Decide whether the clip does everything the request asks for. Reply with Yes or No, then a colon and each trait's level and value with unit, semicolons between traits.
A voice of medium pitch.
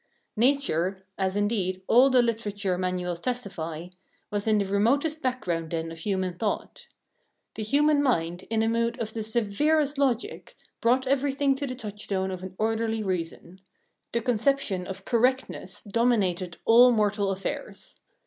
No: high, 215 Hz